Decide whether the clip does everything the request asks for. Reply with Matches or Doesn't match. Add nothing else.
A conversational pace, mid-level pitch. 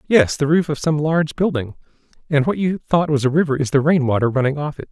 Doesn't match